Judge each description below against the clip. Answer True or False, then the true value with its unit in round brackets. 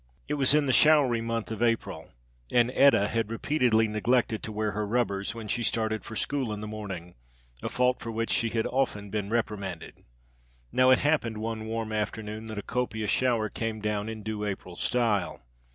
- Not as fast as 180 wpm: False (190 wpm)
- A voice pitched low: True (110 Hz)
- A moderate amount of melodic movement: False (2.2 semitones)